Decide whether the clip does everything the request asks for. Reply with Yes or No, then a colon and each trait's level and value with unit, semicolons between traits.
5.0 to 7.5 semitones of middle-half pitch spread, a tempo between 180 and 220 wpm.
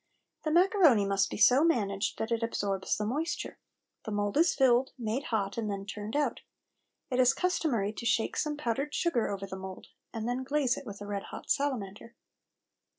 Yes: wide, 5.5 semitones; average, 190 wpm